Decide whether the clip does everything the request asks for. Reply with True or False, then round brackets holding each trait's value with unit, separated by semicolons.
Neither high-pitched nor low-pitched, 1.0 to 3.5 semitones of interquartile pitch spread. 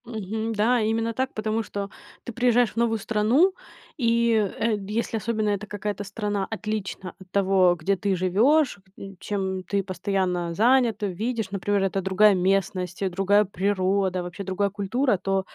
False (205 Hz; 2.8 semitones)